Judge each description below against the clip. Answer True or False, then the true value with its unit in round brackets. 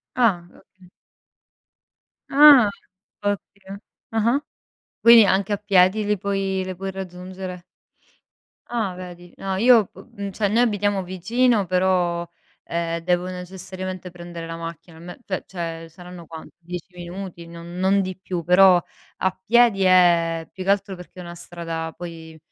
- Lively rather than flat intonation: False (2.4 semitones)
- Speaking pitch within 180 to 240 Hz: True (185 Hz)